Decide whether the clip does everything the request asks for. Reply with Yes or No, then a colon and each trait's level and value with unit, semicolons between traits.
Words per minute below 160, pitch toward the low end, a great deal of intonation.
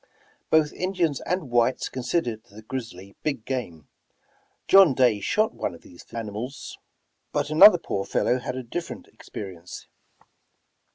Yes: slow, 135 wpm; low, 125 Hz; wide, 6.2 semitones